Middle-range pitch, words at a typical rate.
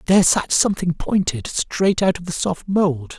Yes: medium, 175 Hz; average, 190 wpm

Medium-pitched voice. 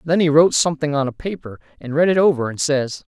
Yes: medium, 150 Hz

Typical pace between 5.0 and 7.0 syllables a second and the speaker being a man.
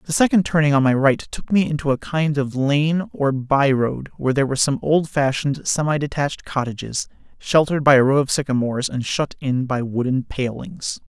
Yes: 5.5 syllables/s; male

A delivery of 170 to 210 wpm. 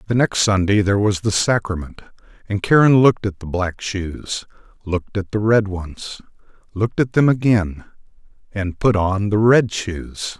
No: average, 160 wpm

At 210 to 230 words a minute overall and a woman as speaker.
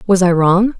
Yes: fast, 225 wpm; female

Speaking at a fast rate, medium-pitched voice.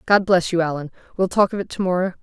Yes: fast, 270 wpm; medium, 180 Hz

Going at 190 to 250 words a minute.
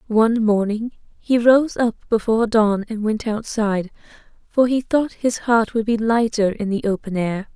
No: average, 175 wpm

